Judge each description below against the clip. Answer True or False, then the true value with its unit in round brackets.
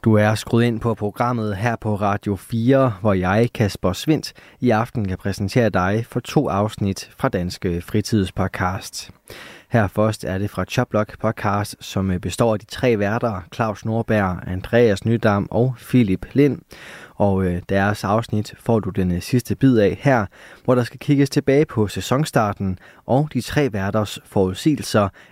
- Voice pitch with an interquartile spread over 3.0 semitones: True (3.8 semitones)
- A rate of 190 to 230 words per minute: False (160 wpm)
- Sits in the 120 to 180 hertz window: False (110 Hz)